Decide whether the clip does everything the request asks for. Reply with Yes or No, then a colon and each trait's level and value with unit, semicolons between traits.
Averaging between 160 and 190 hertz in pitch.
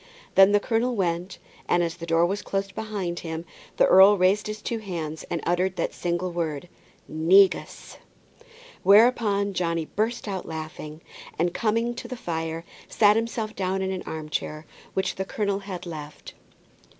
Yes: medium, 185 Hz